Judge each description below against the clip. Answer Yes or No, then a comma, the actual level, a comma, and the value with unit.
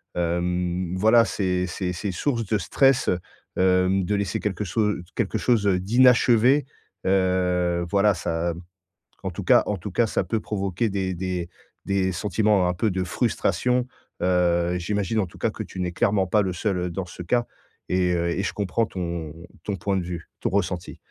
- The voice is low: Yes, very low, 95 Hz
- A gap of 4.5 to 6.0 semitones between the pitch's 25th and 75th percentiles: No, average, 2.8 semitones